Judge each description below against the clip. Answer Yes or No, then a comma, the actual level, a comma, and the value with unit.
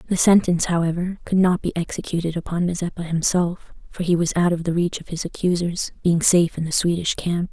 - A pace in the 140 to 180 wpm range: No, fast, 205 wpm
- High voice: No, medium, 175 Hz